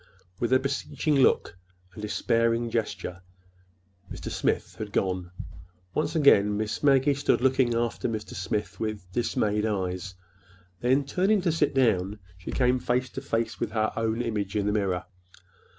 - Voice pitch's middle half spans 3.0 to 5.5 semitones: Yes, average, 4.1 semitones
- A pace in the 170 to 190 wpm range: No, average, 155 wpm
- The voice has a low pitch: Yes, low, 115 Hz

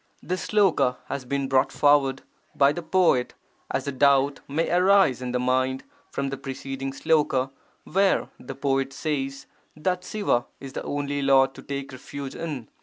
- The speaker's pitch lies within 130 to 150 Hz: Yes, medium, 140 Hz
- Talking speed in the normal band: Yes, average, 165 wpm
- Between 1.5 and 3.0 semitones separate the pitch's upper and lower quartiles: Yes, narrow, 2.5 semitones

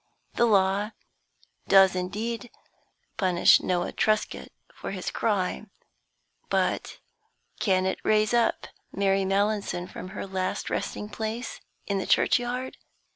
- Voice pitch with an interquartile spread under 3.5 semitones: Yes, narrow, 2.5 semitones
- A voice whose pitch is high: Yes, high, 200 Hz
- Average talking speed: No, slow, 115 wpm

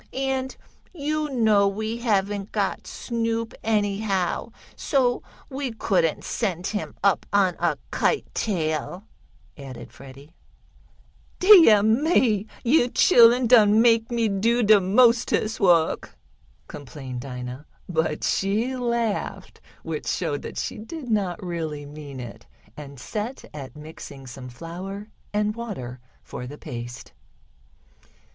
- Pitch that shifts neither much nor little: No, wide, 6.8 semitones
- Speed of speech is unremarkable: No, slow, 120 wpm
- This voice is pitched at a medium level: No, high, 205 Hz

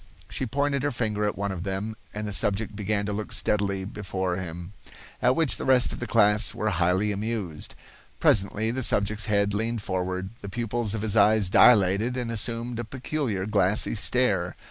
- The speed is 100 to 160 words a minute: No, average, 185 wpm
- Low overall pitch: Yes, low, 105 Hz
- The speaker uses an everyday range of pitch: Yes, average, 3.0 semitones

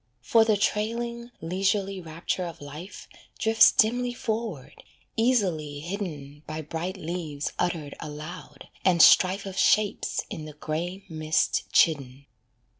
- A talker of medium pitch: Yes, medium, 175 Hz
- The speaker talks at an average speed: No, slow, 120 wpm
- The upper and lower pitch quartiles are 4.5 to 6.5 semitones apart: Yes, average, 5.3 semitones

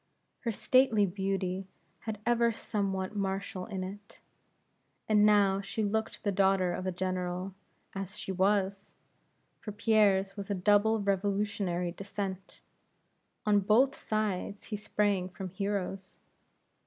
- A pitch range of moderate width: No, narrow, 1.8 semitones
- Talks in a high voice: Yes, high, 200 Hz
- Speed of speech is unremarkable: No, slow, 125 wpm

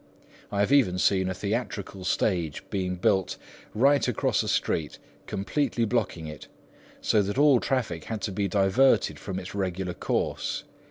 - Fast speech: No, average, 150 wpm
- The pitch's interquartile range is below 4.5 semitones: Yes, average, 3.9 semitones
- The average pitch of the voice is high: No, low, 100 Hz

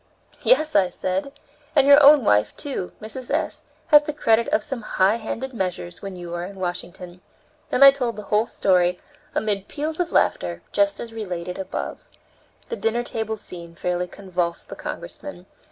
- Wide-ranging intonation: Yes, wide, 7.3 semitones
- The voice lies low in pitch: No, high, 210 Hz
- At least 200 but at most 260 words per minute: No, average, 170 wpm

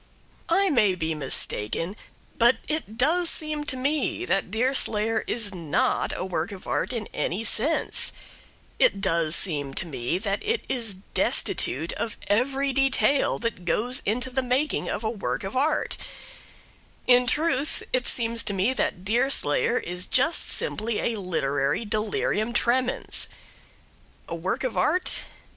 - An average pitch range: No, wide, 6.0 semitones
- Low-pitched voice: No, high, 230 Hz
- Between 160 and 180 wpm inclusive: No, average, 145 wpm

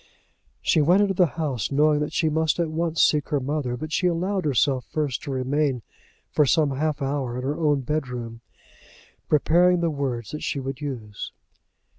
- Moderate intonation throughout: Yes, average, 3.2 semitones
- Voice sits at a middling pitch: Yes, medium, 150 Hz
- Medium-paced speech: Yes, average, 180 wpm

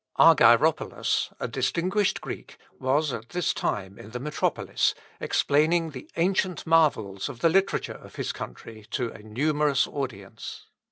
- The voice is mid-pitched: Yes, medium, 145 Hz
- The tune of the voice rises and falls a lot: Yes, wide, 6.8 semitones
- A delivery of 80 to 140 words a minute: Yes, slow, 135 wpm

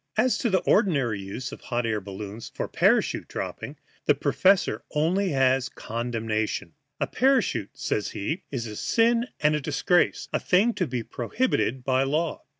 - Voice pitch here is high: No, low, 135 Hz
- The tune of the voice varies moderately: No, wide, 8.8 semitones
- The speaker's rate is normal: Yes, average, 160 wpm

